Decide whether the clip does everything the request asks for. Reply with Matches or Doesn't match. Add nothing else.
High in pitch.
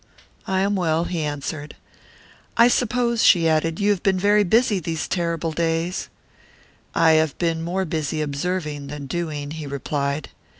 Doesn't match